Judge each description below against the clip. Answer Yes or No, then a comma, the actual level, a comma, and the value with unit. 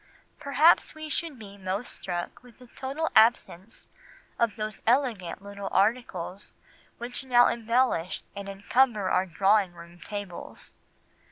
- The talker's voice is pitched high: Yes, high, 215 Hz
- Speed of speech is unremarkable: No, slow, 125 wpm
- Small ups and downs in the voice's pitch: No, average, 4.5 semitones